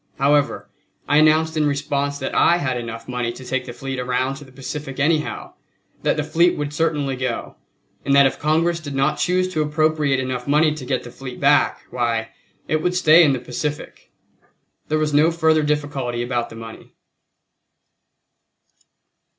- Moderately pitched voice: Yes, medium, 145 Hz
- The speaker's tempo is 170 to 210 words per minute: Yes, average, 175 wpm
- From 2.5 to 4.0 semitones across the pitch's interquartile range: Yes, average, 3.2 semitones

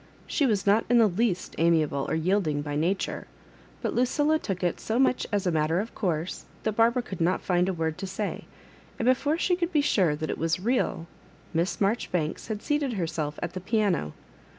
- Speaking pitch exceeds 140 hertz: Yes, high, 190 Hz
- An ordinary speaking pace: No, fast, 210 wpm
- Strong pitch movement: Yes, wide, 5.9 semitones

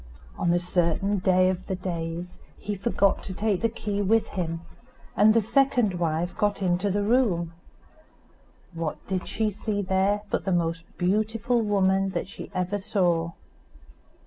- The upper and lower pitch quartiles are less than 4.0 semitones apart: Yes, average, 2.7 semitones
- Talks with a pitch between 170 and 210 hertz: Yes, high, 190 Hz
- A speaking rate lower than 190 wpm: Yes, average, 155 wpm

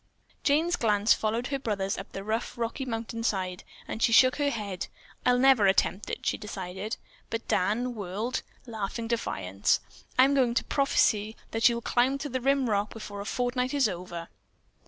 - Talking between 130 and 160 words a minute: No, average, 170 wpm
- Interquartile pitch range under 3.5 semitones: No, average, 3.8 semitones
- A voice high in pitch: Yes, high, 225 Hz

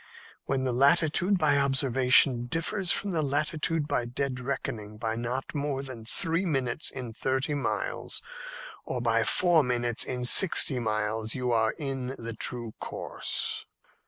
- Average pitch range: Yes, average, 3.6 semitones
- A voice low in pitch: Yes, low, 130 Hz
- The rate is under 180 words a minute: Yes, average, 145 wpm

